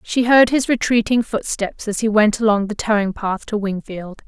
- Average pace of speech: Yes, average, 195 wpm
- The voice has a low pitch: No, high, 215 Hz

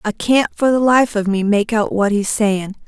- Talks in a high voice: Yes, high, 215 Hz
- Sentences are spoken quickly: Yes, fast, 250 wpm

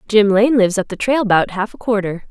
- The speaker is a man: No, female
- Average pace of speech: No, fast, 260 wpm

